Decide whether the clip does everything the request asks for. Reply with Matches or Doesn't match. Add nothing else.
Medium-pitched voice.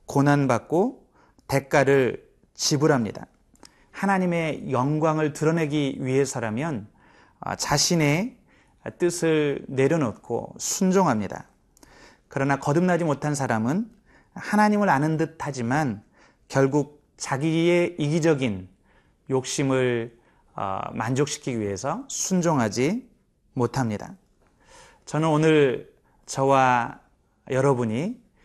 Matches